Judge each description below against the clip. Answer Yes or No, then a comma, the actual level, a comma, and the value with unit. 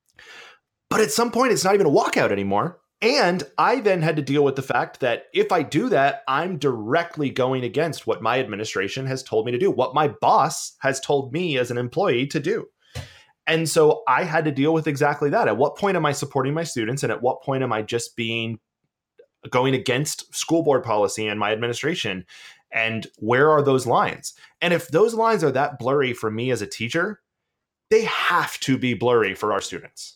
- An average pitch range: No, wide, 5.9 semitones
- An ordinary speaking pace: No, fast, 210 wpm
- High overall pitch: No, medium, 145 Hz